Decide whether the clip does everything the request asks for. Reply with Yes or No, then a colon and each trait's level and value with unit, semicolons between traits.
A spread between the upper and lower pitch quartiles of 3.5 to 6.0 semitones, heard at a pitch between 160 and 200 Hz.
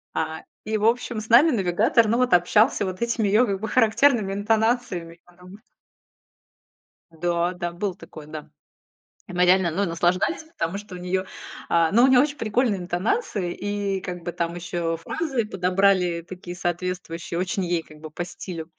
Yes: average, 3.8 semitones; medium, 185 Hz